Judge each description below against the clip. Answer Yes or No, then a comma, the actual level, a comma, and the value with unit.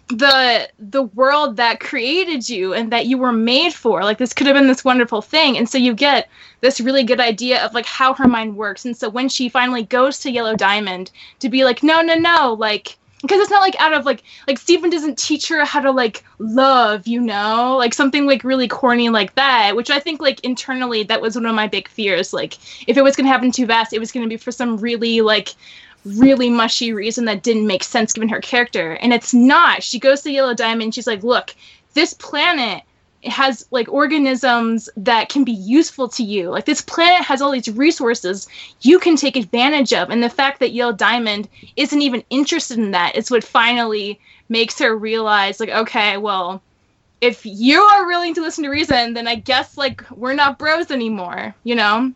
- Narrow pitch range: No, average, 3.3 semitones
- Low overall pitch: No, high, 245 Hz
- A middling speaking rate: No, fast, 215 wpm